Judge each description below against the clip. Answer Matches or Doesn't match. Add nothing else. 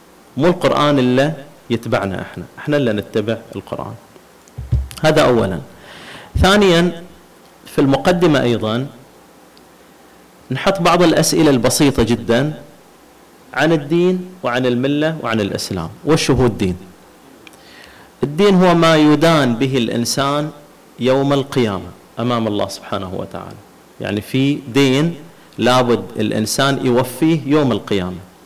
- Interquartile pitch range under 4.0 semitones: Doesn't match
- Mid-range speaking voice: Doesn't match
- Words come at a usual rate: Matches